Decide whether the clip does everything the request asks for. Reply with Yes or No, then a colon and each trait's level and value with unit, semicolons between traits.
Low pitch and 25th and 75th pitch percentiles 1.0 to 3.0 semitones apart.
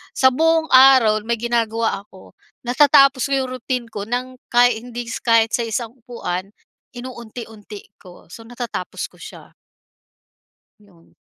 No: high, 240 Hz; narrow, 2.6 semitones